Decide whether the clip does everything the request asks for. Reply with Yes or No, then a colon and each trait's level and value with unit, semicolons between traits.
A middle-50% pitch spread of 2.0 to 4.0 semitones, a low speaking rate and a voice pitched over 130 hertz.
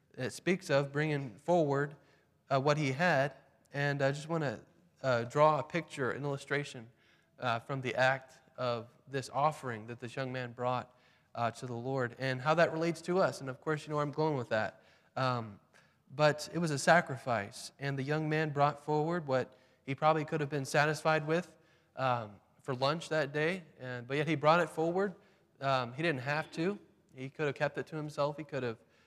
No: average, 3.3 semitones; average, 200 wpm; medium, 140 Hz